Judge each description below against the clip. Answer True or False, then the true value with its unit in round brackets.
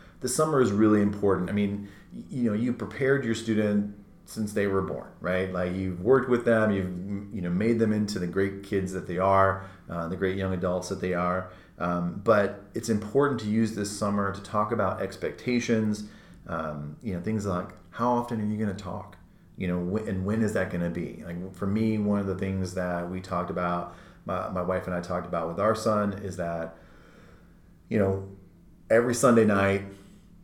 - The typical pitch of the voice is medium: False (100 Hz)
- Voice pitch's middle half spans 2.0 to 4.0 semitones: True (3.1 semitones)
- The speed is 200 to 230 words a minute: True (205 wpm)